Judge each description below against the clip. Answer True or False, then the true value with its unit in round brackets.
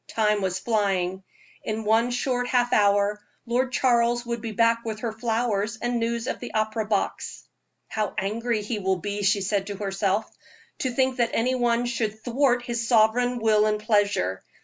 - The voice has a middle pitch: False (220 Hz)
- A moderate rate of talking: True (175 wpm)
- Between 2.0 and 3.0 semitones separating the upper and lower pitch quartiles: True (2.6 semitones)